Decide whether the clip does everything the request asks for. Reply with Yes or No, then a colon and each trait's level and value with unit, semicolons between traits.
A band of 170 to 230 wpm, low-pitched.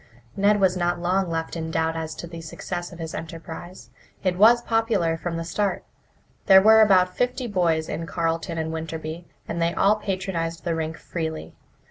No: average, 180 wpm; medium, 170 Hz